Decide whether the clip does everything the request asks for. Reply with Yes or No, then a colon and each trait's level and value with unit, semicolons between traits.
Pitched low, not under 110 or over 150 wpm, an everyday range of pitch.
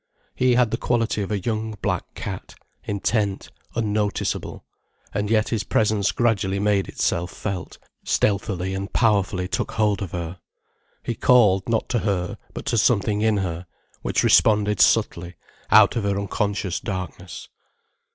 No: low, 105 Hz; average, 145 wpm; narrow, 2.3 semitones